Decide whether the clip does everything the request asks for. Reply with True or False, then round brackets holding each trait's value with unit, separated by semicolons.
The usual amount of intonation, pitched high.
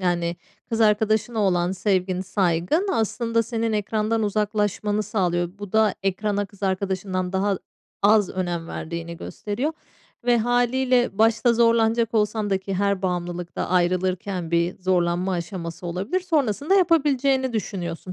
True (3.8 semitones; 205 Hz)